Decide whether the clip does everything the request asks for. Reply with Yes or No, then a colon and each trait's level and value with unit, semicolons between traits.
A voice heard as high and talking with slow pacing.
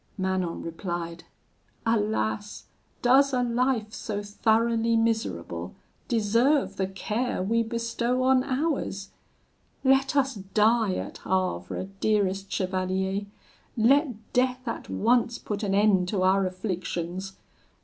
Yes: high, 215 Hz; slow, 110 wpm